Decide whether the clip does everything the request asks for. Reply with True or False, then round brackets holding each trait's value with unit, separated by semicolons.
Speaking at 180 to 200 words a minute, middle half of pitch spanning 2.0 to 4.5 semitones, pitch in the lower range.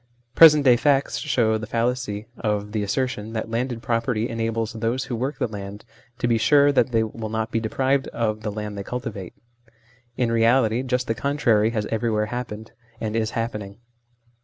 True (185 wpm; 2.5 semitones; 115 Hz)